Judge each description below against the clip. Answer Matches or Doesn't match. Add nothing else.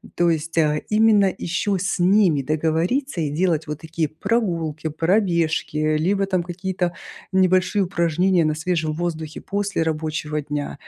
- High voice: Doesn't match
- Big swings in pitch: Doesn't match